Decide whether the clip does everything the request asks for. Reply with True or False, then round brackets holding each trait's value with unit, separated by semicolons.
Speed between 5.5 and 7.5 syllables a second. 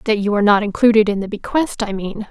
True (6.5 syllables/s)